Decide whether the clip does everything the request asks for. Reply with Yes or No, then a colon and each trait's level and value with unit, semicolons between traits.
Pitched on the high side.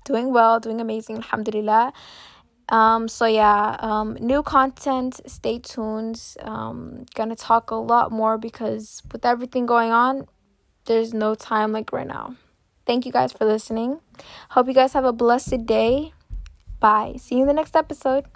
Yes: high, 230 Hz